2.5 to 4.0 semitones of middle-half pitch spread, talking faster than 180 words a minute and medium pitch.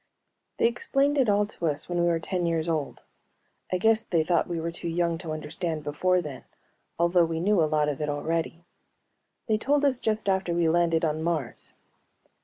Yes: average, 3.0 semitones; average, 200 wpm; medium, 170 Hz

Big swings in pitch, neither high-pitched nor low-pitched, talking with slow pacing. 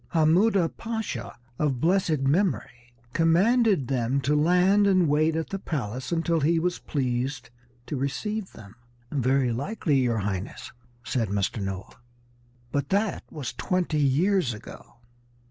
Yes: wide, 6.5 semitones; medium, 150 Hz; slow, 130 wpm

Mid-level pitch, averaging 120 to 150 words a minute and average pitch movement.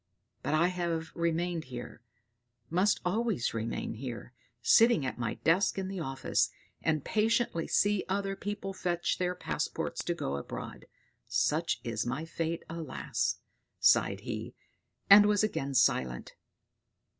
No: medium, 165 Hz; slow, 135 wpm; wide, 6.9 semitones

